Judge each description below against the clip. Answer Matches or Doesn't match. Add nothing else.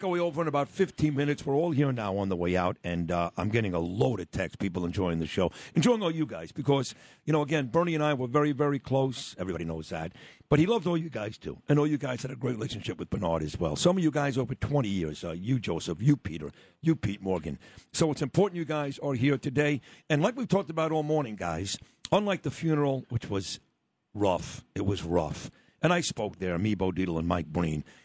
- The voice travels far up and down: Matches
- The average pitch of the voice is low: Matches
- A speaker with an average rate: Doesn't match